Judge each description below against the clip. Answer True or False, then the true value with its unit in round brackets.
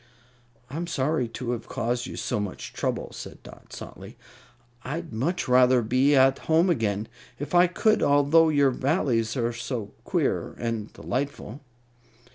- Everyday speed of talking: True (145 wpm)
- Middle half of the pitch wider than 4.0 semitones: True (4.5 semitones)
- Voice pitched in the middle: False (130 Hz)